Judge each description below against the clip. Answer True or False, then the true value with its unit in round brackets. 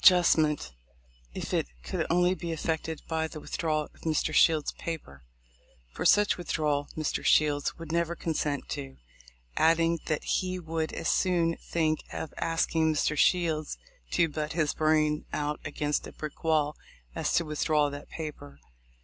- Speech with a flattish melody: True (1.7 semitones)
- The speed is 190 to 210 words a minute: False (160 wpm)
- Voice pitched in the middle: True (155 Hz)